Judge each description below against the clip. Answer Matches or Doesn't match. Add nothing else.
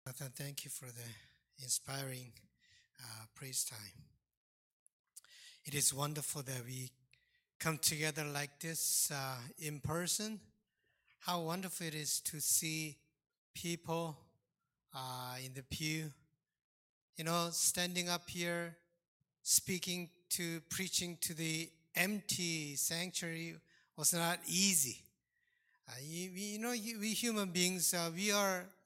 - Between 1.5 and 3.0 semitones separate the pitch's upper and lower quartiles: Doesn't match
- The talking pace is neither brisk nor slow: Doesn't match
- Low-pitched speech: Doesn't match